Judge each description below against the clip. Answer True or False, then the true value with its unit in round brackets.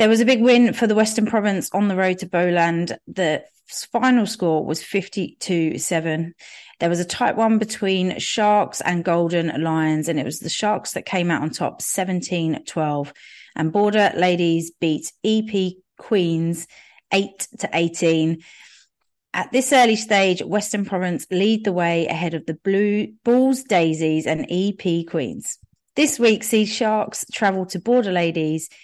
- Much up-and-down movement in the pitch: False (4.2 semitones)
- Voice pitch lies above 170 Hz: True (185 Hz)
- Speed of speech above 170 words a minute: False (160 wpm)